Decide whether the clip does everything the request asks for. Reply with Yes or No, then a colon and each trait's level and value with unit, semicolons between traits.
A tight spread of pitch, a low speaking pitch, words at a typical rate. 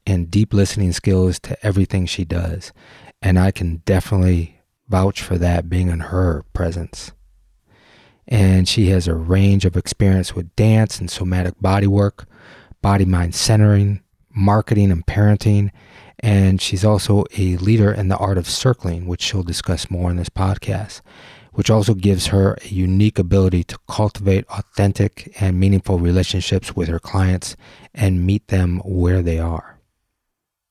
Yes: narrow, 2.3 semitones; very low, 95 Hz; average, 150 wpm